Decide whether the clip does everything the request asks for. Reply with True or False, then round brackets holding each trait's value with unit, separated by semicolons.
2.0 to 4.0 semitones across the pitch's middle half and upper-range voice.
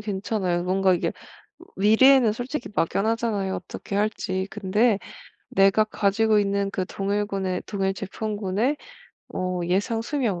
True (2.4 semitones; 200 Hz)